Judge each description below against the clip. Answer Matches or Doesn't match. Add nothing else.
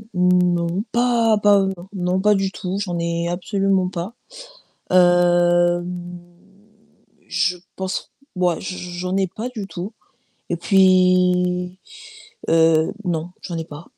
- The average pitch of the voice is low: Doesn't match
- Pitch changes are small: Matches